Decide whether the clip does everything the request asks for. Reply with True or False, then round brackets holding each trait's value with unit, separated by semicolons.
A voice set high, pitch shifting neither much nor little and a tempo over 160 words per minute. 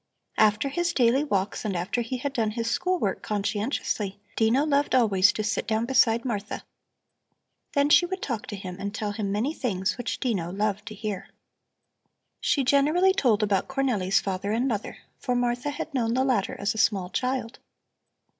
True (225 Hz; 4.5 semitones; 180 wpm)